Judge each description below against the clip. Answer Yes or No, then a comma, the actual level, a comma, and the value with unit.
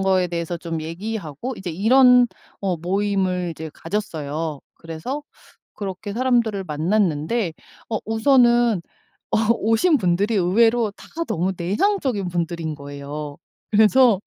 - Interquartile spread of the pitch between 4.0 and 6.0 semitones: Yes, average, 5.3 semitones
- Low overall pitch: No, high, 190 Hz